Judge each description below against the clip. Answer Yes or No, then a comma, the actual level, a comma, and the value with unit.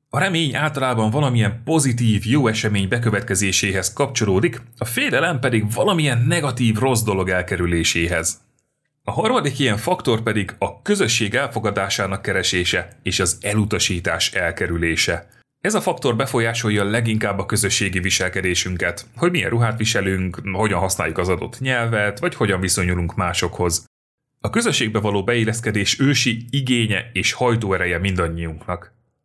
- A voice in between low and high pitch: No, low, 110 Hz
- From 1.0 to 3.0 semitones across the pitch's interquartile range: No, average, 4.7 semitones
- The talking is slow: No, average, 125 wpm